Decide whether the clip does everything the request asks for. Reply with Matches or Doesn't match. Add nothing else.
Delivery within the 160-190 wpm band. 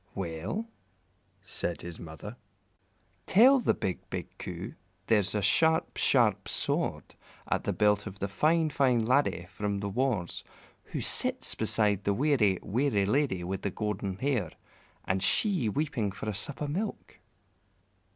Doesn't match